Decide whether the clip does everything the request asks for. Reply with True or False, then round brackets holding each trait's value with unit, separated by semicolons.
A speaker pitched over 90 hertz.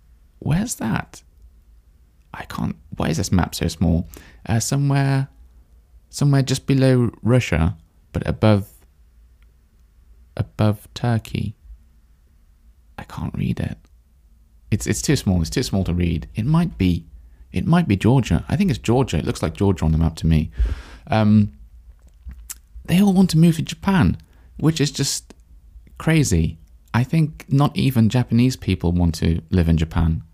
False (85 Hz)